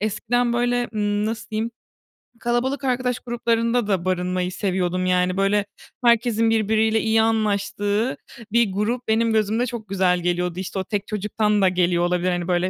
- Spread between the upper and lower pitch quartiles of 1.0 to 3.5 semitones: No, average, 3.9 semitones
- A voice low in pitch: No, high, 210 Hz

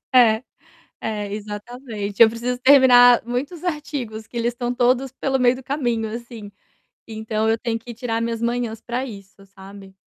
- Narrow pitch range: Yes, narrow, 2.2 semitones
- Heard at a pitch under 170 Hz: No, high, 235 Hz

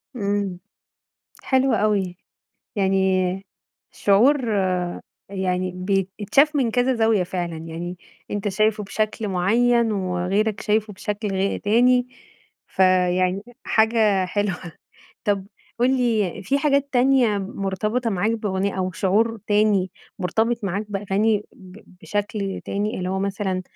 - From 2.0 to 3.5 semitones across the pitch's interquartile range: Yes, average, 2.9 semitones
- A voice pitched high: Yes, high, 205 Hz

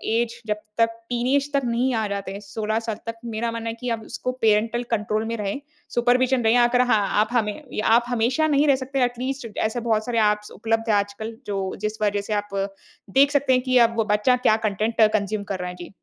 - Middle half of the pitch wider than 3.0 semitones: No, average, 2.7 semitones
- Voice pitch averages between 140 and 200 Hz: No, high, 230 Hz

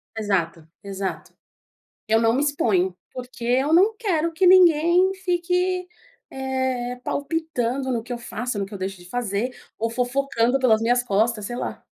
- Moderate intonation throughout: No, wide, 5.7 semitones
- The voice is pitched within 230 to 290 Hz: Yes, high, 245 Hz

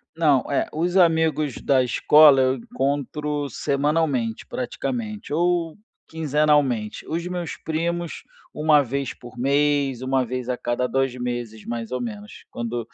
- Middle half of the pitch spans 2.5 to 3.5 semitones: No, average, 4.1 semitones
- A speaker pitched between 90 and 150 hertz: Yes, medium, 140 Hz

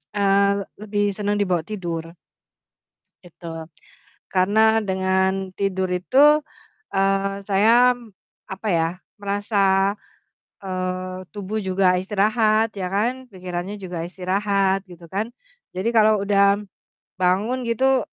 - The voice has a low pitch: No, high, 195 Hz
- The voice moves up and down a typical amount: No, narrow, 2.2 semitones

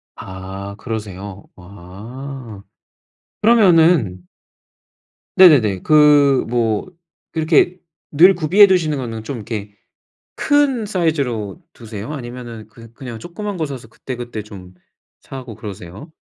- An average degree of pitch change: No, wide, 7.1 semitones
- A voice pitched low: Yes, low, 120 Hz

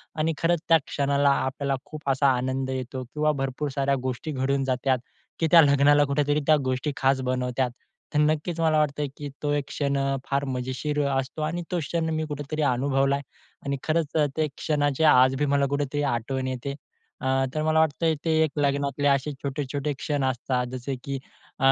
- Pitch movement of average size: No, narrow, 2.2 semitones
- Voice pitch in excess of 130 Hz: Yes, medium, 140 Hz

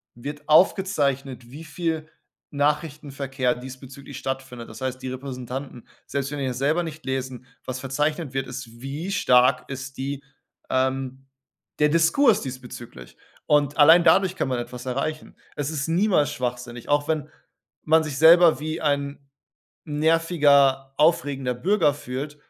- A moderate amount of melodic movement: Yes, average, 3.0 semitones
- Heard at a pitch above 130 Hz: Yes, medium, 140 Hz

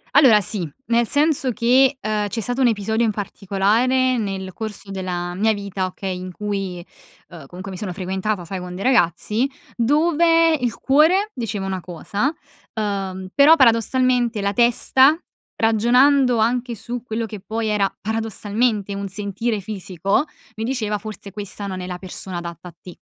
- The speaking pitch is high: Yes, high, 215 Hz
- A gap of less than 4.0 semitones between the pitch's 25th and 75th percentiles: No, average, 4.3 semitones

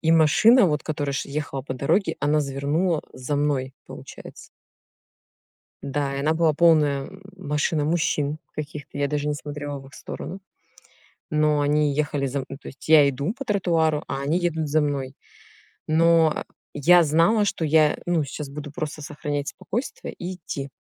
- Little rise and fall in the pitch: Yes, narrow, 2.3 semitones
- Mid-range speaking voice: Yes, medium, 150 Hz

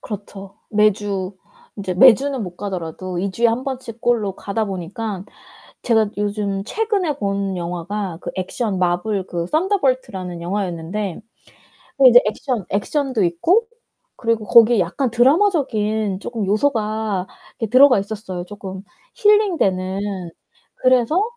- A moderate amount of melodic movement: Yes, average, 4.3 semitones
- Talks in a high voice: Yes, high, 210 Hz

